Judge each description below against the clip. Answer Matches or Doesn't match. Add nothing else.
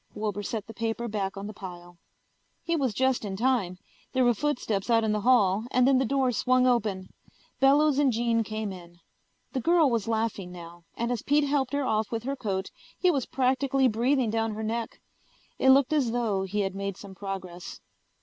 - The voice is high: Matches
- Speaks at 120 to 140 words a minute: Doesn't match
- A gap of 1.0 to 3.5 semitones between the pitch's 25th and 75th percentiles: Doesn't match